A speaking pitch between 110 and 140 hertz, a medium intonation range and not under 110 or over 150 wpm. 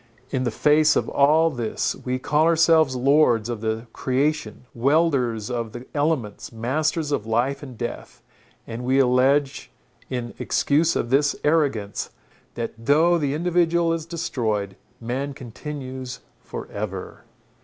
Yes: low, 135 Hz; average, 4.4 semitones; slow, 135 wpm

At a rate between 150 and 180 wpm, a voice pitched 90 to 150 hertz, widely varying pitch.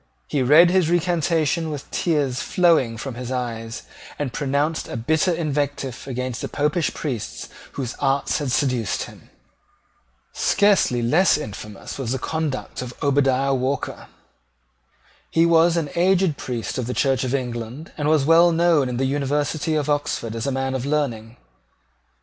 No: average, 155 wpm; medium, 140 Hz; average, 4.0 semitones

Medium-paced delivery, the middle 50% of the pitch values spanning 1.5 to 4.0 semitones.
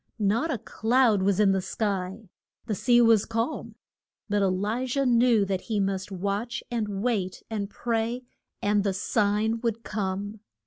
Yes: average, 165 wpm; average, 2.8 semitones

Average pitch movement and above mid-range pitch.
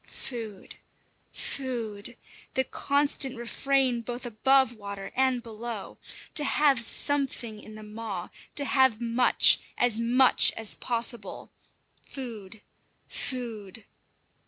Yes: average, 3.3 semitones; high, 235 Hz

